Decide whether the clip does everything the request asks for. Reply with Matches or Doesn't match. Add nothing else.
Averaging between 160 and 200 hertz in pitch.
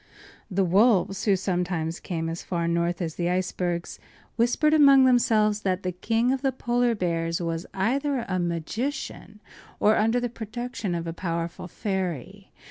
Matches